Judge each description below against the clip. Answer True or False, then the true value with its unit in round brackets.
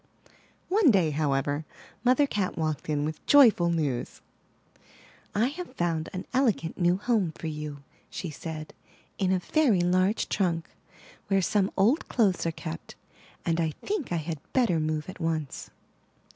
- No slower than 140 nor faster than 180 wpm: True (155 wpm)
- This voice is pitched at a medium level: True (175 Hz)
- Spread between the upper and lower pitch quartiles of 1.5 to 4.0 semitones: False (5.3 semitones)